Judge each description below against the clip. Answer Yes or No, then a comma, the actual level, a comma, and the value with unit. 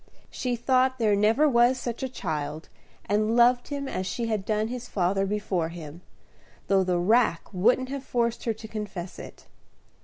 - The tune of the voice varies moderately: Yes, average, 4.6 semitones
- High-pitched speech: Yes, high, 220 Hz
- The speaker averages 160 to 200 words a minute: Yes, average, 175 wpm